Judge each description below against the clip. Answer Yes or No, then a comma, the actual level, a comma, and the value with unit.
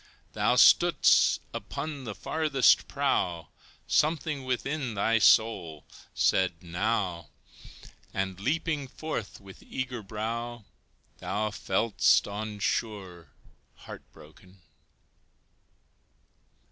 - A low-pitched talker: Yes, low, 110 Hz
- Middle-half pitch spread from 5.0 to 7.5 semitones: Yes, wide, 5.4 semitones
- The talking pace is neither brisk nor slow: No, slow, 85 wpm